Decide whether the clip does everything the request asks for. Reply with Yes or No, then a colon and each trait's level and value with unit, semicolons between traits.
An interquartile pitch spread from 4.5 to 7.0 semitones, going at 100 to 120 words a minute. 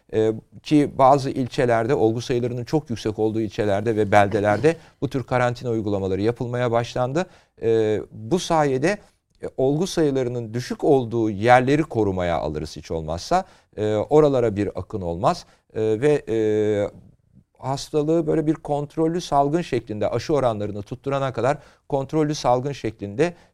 Yes: average, 5.1 semitones; average, 115 wpm